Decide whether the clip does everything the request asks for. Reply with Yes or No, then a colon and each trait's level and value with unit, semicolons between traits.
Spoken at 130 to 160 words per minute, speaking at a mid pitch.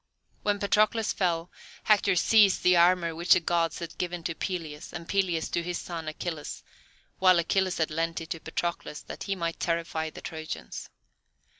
No: average, 170 wpm; medium, 170 Hz